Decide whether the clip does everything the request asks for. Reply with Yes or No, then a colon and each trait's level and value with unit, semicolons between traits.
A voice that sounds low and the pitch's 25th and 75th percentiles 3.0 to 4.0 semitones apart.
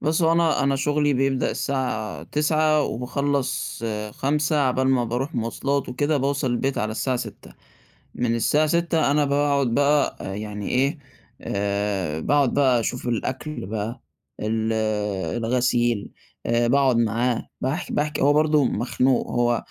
Yes: low, 130 Hz; average, 3.7 semitones